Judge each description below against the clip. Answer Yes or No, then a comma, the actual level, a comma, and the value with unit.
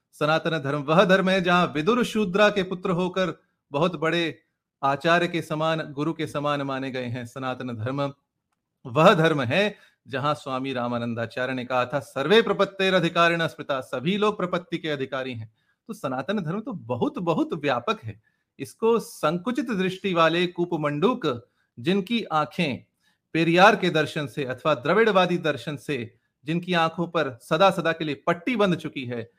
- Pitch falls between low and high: Yes, medium, 160 Hz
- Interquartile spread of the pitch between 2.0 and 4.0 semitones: No, average, 4.9 semitones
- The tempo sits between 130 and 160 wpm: Yes, average, 155 wpm